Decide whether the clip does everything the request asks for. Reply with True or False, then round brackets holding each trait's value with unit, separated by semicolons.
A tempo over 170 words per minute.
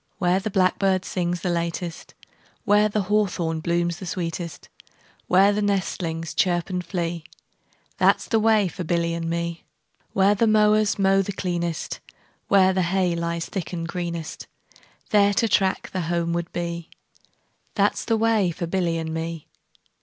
False (165 wpm)